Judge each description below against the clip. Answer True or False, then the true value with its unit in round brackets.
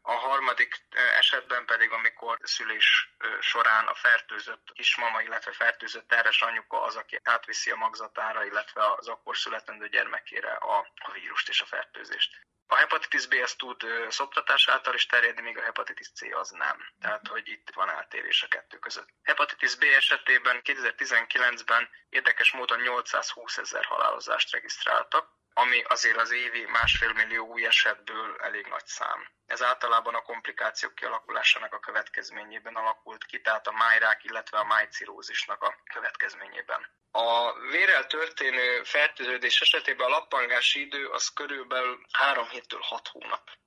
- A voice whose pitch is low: False (395 Hz)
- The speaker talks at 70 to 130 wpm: False (145 wpm)